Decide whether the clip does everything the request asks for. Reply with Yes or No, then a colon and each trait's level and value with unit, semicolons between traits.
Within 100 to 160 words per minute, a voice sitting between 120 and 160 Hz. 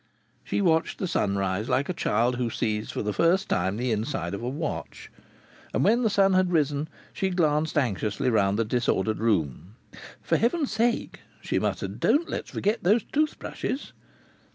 No: average, 175 wpm; medium, 140 Hz